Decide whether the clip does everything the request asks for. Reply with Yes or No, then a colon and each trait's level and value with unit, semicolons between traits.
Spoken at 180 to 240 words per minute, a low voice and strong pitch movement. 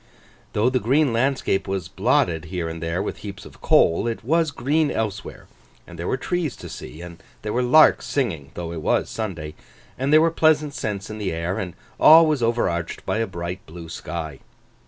Yes: average, 200 wpm; low, 105 Hz; wide, 7.7 semitones